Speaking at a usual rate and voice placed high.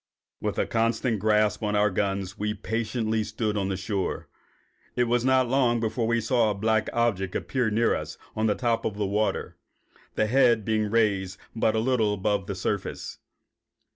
No: average, 175 wpm; low, 110 Hz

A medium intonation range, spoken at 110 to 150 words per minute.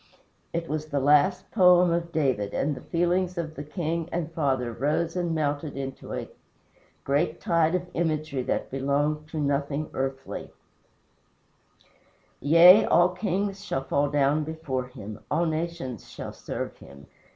Yes: average, 3.5 semitones; average, 145 wpm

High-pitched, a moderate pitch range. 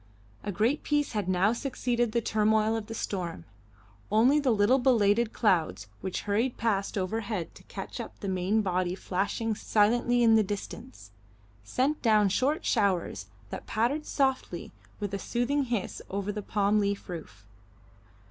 Yes: high, 215 Hz; average, 3.6 semitones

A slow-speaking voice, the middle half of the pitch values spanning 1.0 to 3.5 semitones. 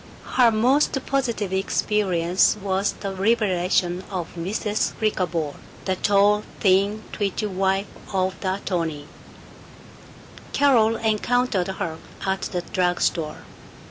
Yes: slow, 110 wpm; average, 2.9 semitones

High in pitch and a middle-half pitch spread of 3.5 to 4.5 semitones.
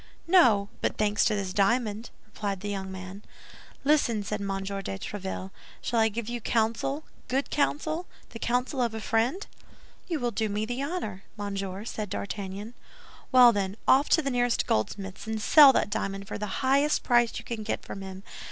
Yes: high, 220 Hz; average, 3.8 semitones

